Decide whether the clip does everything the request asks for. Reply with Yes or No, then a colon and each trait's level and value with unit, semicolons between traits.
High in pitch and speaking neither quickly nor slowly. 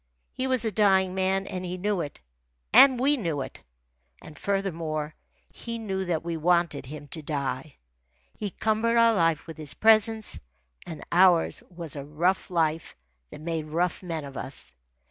No: medium, 175 Hz; average, 165 wpm